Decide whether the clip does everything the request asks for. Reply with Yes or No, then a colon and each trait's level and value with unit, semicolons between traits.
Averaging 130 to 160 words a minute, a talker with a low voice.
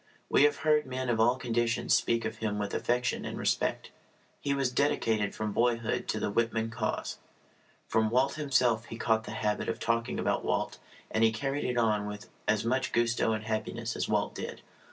No: average, 195 wpm; low, 115 Hz